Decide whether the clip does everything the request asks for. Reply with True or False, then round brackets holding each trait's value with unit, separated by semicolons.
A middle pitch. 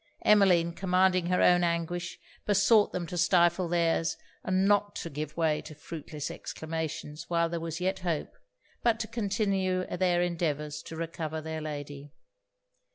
True (170 Hz)